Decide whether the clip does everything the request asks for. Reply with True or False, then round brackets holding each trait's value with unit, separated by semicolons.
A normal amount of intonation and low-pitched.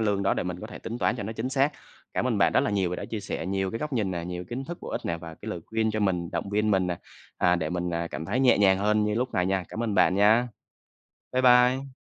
True (4.6 semitones; 105 Hz)